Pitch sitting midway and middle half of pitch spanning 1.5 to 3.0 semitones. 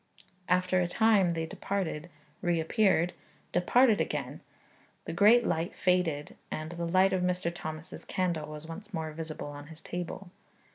Yes: medium, 175 Hz; narrow, 2.6 semitones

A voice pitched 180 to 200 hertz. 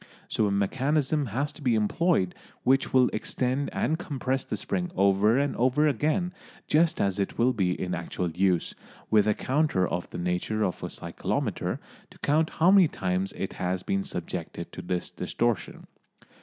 No: low, 120 Hz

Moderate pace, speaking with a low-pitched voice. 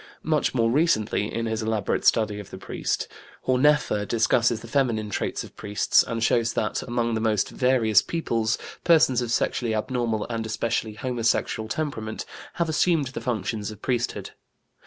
Yes: average, 155 wpm; low, 115 Hz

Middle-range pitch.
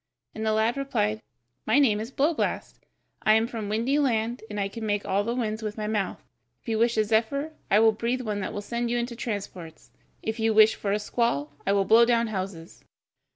No: high, 220 Hz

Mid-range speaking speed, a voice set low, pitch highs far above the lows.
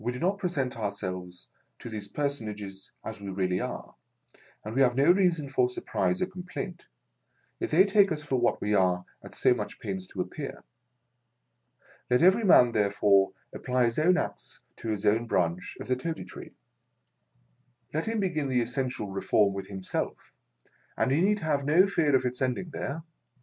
Yes: average, 175 wpm; low, 125 Hz; wide, 8.3 semitones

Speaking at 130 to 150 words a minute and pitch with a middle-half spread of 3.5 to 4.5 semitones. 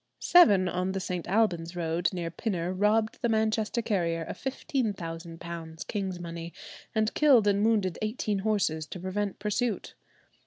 Yes: average, 145 wpm; average, 4.2 semitones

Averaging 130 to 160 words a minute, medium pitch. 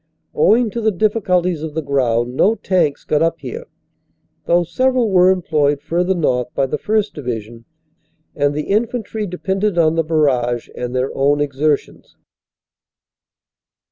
Yes: average, 140 wpm; medium, 165 Hz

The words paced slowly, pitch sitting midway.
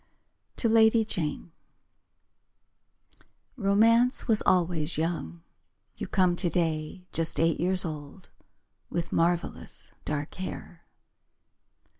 Yes: slow, 90 wpm; medium, 175 Hz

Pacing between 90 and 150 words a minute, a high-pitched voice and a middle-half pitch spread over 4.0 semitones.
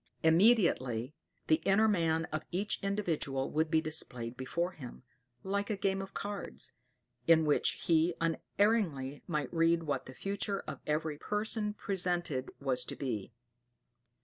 No: average, 140 wpm; medium, 165 Hz; average, 5.2 semitones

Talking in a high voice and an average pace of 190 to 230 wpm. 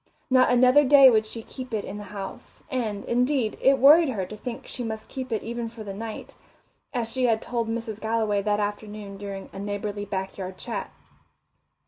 Yes: high, 220 Hz; average, 195 wpm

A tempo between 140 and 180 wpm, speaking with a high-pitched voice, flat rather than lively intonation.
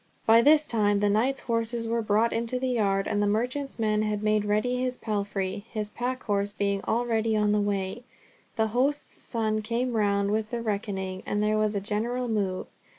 No: average, 195 wpm; high, 215 Hz; narrow, 2.3 semitones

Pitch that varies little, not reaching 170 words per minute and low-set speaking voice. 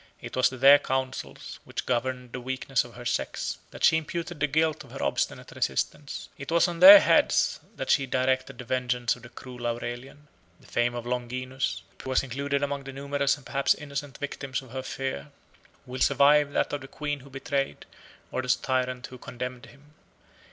No: narrow, 2.1 semitones; average, 195 wpm; low, 130 Hz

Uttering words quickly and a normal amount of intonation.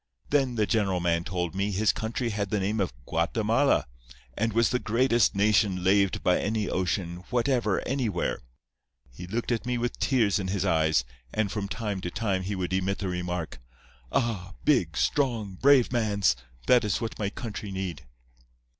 No: average, 170 wpm; average, 3.9 semitones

